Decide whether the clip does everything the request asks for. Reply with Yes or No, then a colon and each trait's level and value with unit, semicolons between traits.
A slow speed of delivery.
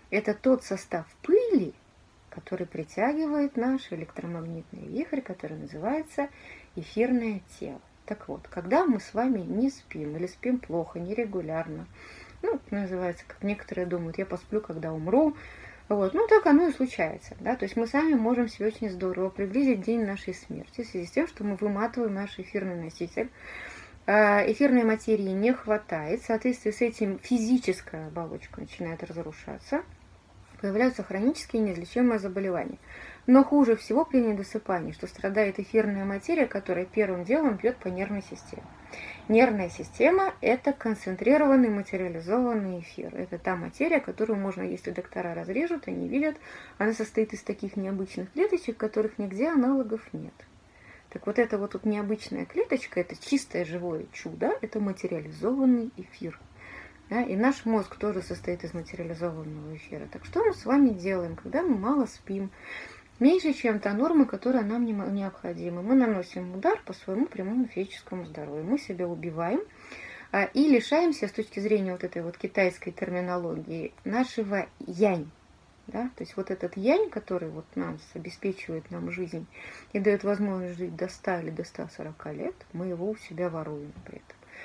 No: average, 150 wpm